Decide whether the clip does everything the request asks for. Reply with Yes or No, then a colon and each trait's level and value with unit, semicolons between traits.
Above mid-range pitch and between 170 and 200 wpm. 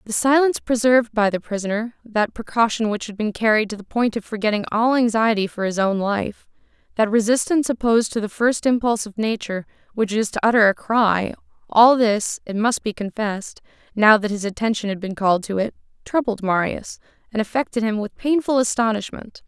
Yes: high, 220 Hz; average, 190 wpm